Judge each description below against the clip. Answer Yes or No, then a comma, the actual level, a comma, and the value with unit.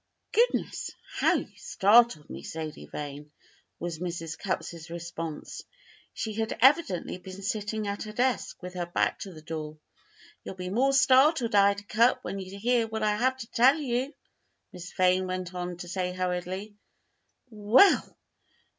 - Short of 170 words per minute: Yes, average, 155 wpm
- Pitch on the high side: Yes, high, 195 Hz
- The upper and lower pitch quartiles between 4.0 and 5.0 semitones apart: Yes, average, 4.6 semitones